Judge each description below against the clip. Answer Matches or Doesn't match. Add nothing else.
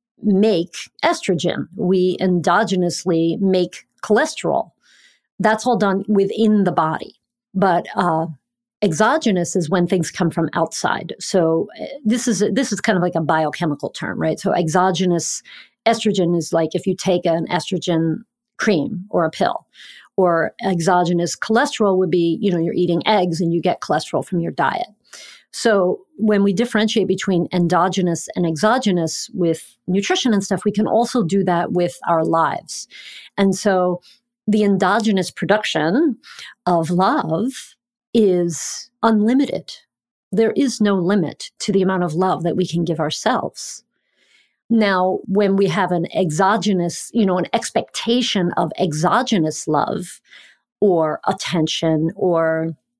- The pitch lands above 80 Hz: Matches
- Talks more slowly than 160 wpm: Matches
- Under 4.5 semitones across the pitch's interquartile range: Matches